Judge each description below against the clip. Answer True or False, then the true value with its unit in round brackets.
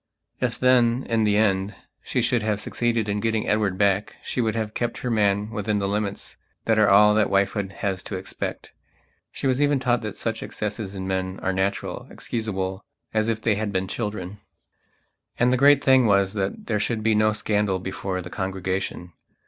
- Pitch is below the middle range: True (105 Hz)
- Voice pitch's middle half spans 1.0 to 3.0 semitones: True (2.6 semitones)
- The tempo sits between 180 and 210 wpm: True (190 wpm)